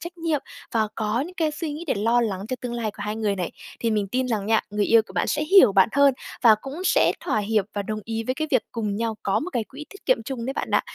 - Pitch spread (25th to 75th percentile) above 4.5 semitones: Yes, average, 5.2 semitones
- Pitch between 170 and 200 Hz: No, high, 230 Hz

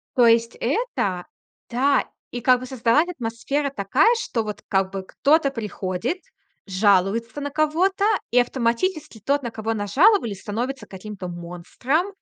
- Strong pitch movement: Yes, wide, 5.7 semitones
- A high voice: Yes, high, 235 Hz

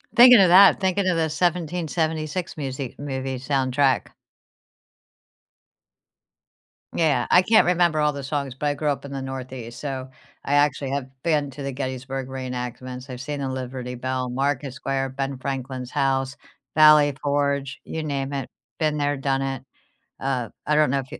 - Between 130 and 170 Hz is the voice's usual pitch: Yes, medium, 140 Hz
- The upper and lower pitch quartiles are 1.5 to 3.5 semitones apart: Yes, narrow, 2.4 semitones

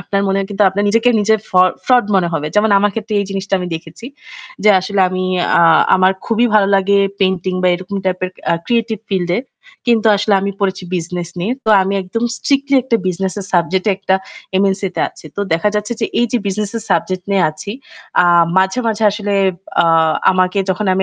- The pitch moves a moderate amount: No, narrow, 2.3 semitones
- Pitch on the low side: No, high, 195 Hz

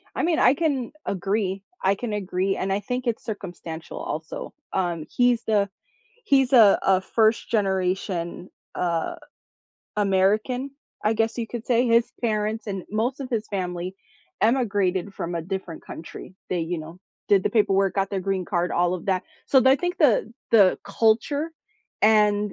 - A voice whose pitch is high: Yes, high, 205 Hz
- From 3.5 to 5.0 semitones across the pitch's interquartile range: Yes, average, 3.8 semitones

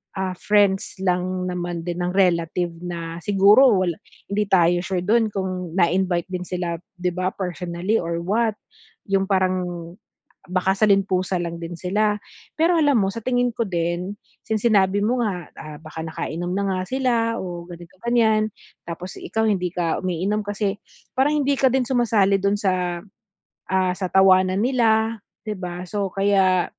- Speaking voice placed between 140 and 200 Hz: Yes, high, 190 Hz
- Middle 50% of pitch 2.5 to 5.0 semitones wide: Yes, average, 2.9 semitones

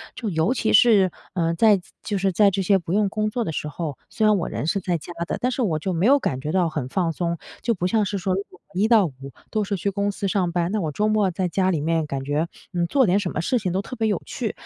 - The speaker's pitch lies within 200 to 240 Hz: No, high, 190 Hz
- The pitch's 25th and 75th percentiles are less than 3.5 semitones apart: No, average, 3.8 semitones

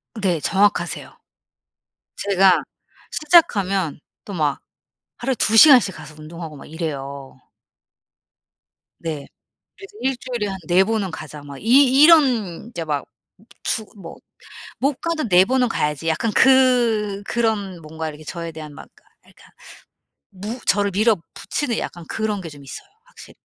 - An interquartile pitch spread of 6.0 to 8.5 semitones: Yes, wide, 6.9 semitones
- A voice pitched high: Yes, high, 195 Hz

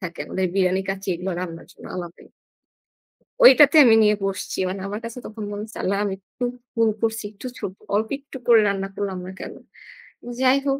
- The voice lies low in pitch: No, high, 205 Hz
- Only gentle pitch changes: No, average, 3.2 semitones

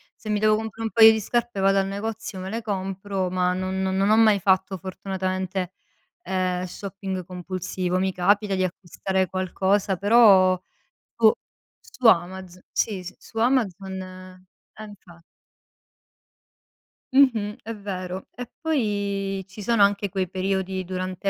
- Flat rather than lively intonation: Yes, narrow, 2.1 semitones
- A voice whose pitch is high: Yes, high, 195 Hz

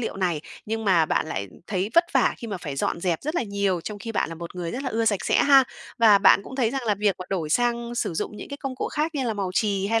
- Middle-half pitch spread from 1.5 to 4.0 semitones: No, average, 4.7 semitones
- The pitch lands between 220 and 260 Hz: No, high, 210 Hz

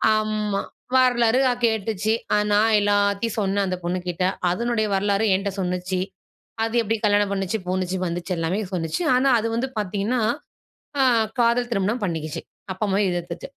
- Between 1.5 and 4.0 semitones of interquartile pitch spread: Yes, average, 3.4 semitones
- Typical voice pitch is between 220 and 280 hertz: No, high, 200 Hz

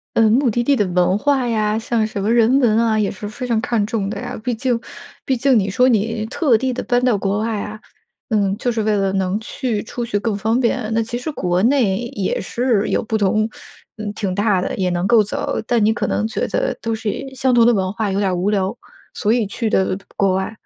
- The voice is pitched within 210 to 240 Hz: Yes, high, 220 Hz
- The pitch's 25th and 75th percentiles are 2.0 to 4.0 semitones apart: Yes, average, 3.0 semitones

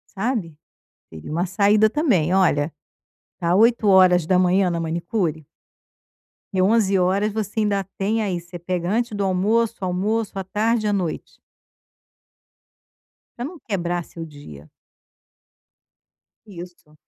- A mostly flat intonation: No, average, 3.6 semitones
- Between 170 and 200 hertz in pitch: Yes, high, 190 Hz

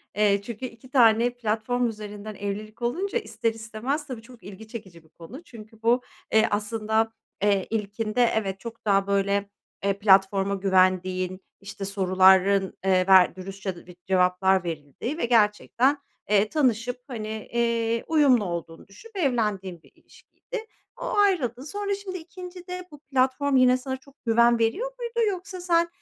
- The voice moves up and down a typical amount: Yes, average, 4.8 semitones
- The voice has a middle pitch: No, high, 225 Hz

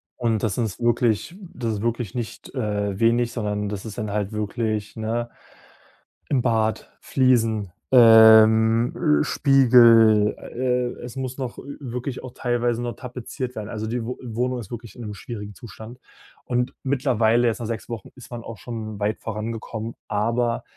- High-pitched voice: No, low, 115 Hz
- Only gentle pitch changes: Yes, narrow, 2.1 semitones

